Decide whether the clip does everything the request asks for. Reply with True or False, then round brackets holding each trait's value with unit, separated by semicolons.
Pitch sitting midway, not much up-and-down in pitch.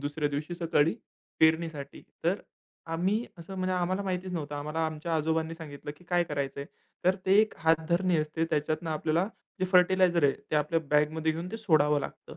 False (160 Hz; 3.0 semitones)